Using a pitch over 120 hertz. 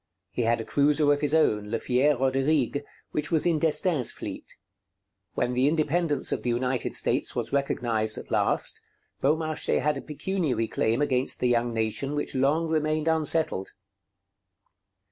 Yes: medium, 140 Hz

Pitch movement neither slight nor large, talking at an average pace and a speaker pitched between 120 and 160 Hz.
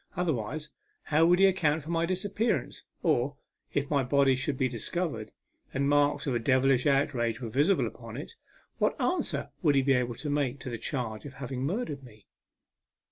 Yes: average, 3.7 semitones; average, 185 wpm; medium, 140 Hz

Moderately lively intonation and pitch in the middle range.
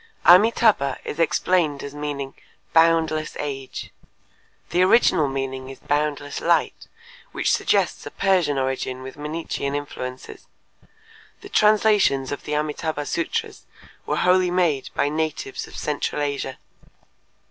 Yes: average, 3.8 semitones; medium, 150 Hz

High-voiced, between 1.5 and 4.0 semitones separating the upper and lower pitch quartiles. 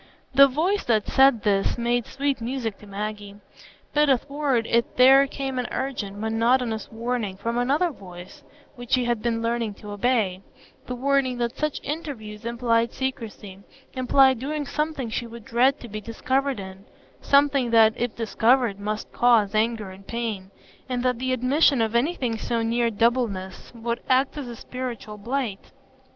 Yes: high, 235 Hz; average, 3.3 semitones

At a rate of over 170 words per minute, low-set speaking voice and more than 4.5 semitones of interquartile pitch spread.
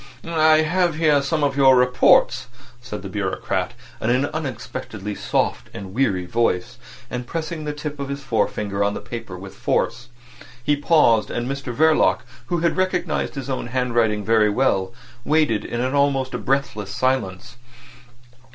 No: average, 155 wpm; low, 130 Hz; wide, 5.4 semitones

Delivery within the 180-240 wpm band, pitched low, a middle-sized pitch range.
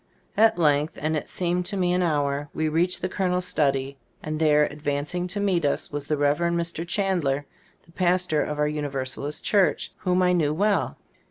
No: average, 190 wpm; medium, 160 Hz; average, 3.6 semitones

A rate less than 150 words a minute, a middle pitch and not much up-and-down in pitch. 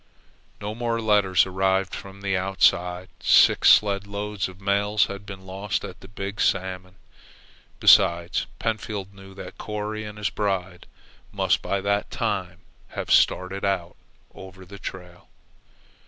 No: slow, 135 wpm; very low, 95 Hz; narrow, 1.6 semitones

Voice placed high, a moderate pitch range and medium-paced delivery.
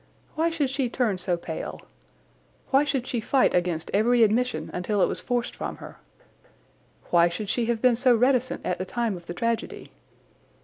Yes: high, 235 Hz; average, 5.0 semitones; average, 180 wpm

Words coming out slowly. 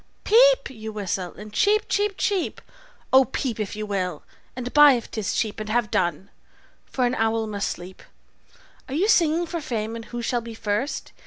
No: average, 185 wpm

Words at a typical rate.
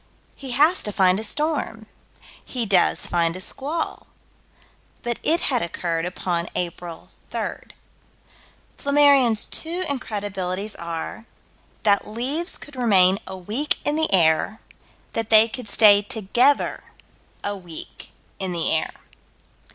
No: slow, 125 wpm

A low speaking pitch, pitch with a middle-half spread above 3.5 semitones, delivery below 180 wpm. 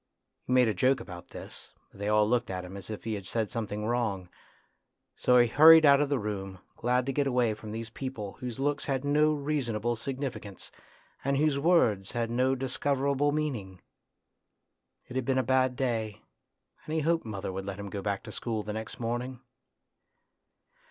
No: low, 120 Hz; average, 4.4 semitones; average, 190 wpm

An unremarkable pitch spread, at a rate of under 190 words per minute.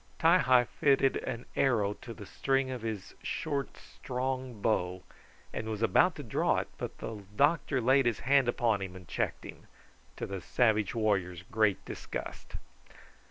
Yes: average, 4.2 semitones; average, 160 wpm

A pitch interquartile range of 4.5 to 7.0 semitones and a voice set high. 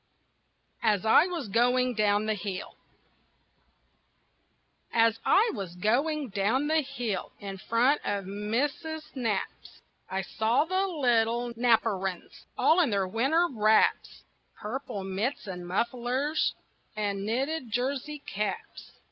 Yes: average, 5.1 semitones; high, 230 Hz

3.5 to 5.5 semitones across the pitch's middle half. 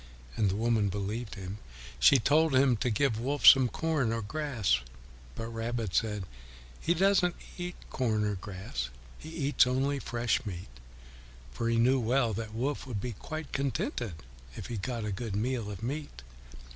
Yes: average, 4.6 semitones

